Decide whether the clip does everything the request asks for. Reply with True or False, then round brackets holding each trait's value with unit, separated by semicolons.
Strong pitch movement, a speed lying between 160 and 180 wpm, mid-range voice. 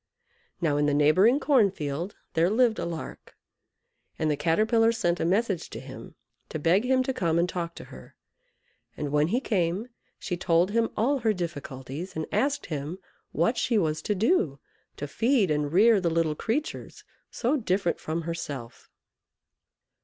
True (6.2 semitones; 170 wpm; 175 Hz)